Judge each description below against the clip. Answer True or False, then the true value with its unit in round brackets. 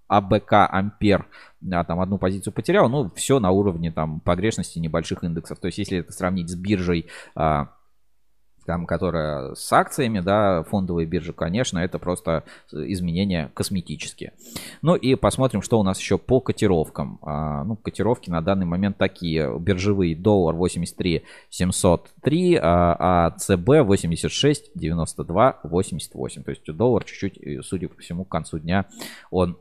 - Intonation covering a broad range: False (3.4 semitones)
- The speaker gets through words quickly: False (145 wpm)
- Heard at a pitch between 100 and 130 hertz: False (90 Hz)